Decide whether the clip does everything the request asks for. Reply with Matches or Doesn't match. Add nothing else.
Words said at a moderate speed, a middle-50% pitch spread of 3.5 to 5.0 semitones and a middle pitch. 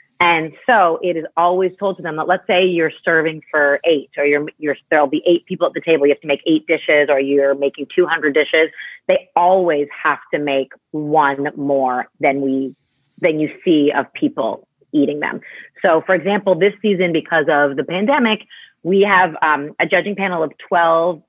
Matches